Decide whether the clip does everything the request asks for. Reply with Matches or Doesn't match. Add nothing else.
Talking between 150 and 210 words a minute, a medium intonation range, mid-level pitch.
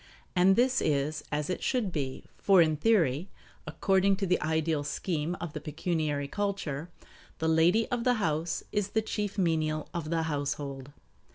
Matches